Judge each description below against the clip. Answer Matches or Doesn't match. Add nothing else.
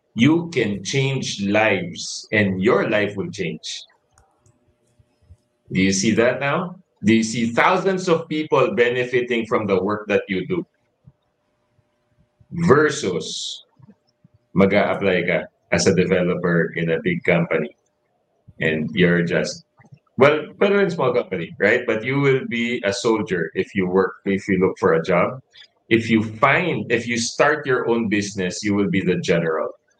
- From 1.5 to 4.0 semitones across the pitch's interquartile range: Doesn't match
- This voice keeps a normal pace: Matches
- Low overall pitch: Matches